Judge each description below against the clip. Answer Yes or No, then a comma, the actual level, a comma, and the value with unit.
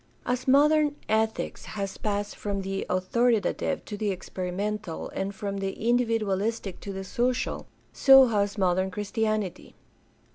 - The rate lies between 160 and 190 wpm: No, slow, 135 wpm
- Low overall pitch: No, high, 205 Hz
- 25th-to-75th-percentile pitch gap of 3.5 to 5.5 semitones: No, average, 2.9 semitones